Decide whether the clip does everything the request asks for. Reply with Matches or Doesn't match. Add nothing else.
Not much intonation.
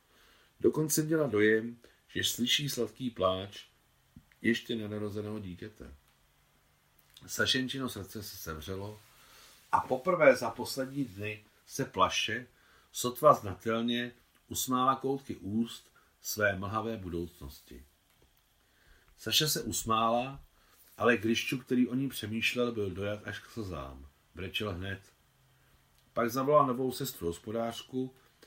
Doesn't match